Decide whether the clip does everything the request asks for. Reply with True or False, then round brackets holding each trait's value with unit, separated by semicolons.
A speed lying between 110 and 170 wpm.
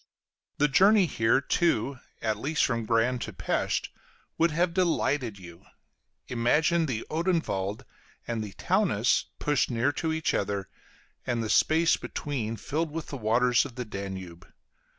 True (145 wpm)